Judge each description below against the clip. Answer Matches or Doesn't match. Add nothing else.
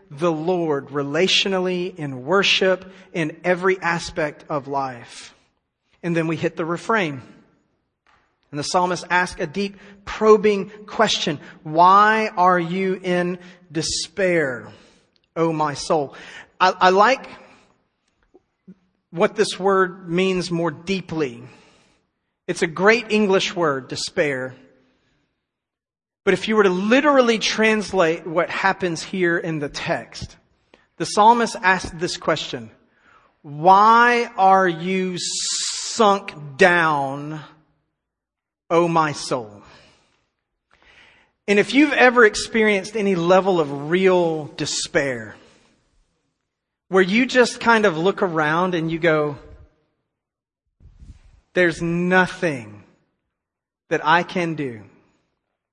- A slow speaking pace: Matches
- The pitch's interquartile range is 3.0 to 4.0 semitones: Matches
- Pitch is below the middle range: Doesn't match